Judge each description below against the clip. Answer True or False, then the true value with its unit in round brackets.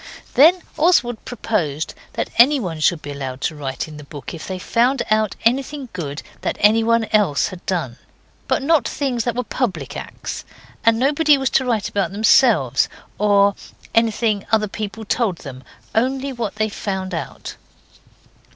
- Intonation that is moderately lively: False (6.1 semitones)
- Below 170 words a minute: True (160 wpm)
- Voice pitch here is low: False (215 Hz)